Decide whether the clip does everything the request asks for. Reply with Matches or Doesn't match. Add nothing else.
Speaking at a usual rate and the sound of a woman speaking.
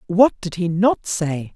Matches